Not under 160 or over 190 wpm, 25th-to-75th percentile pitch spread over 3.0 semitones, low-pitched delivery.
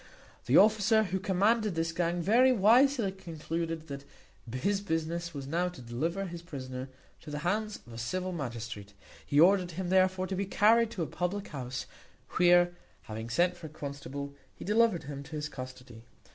No: average, 175 wpm; wide, 5.6 semitones; medium, 170 Hz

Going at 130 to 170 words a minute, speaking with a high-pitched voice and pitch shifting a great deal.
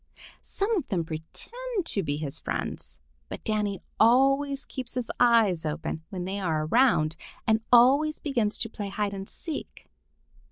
Yes: average, 155 wpm; high, 220 Hz; wide, 6.9 semitones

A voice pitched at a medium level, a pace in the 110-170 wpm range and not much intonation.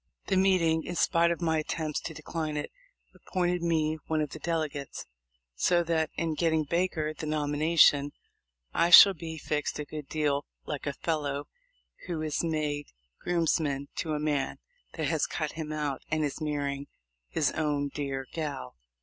Yes: medium, 155 Hz; average, 165 wpm; narrow, 2.1 semitones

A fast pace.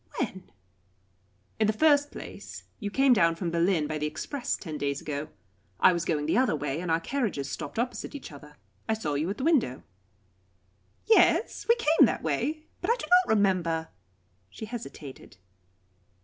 No: average, 175 wpm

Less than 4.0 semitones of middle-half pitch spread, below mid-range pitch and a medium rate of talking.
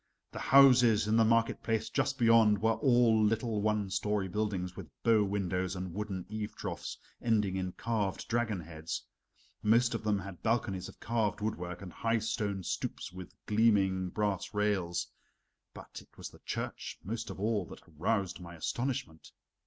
Yes: average, 3.3 semitones; low, 105 Hz; average, 165 wpm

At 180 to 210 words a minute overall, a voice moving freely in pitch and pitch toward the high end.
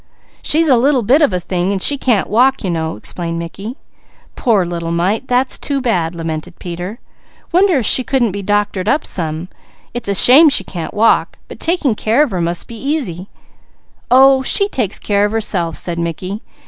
Yes: average, 185 wpm; wide, 6.9 semitones; high, 210 Hz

